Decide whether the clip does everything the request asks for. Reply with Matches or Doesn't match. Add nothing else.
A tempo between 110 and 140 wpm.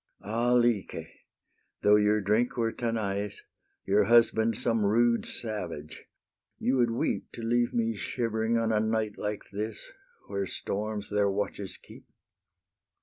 Matches